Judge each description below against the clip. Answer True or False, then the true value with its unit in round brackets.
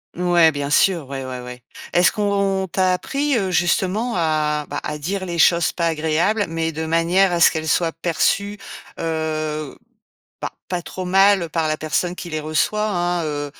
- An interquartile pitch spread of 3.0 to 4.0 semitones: True (3.3 semitones)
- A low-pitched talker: False (170 Hz)